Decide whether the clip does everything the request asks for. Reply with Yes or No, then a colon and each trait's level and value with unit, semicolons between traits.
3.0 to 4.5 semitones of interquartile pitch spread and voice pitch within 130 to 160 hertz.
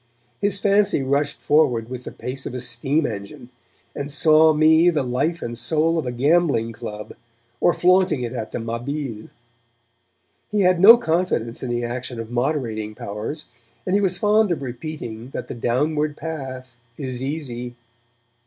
No: average, 5.0 semitones; low, 135 Hz